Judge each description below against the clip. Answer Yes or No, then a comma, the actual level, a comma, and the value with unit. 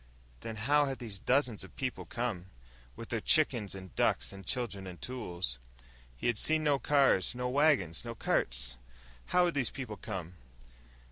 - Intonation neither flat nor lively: No, wide, 6.0 semitones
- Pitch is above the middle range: No, low, 115 Hz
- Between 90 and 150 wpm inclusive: No, average, 165 wpm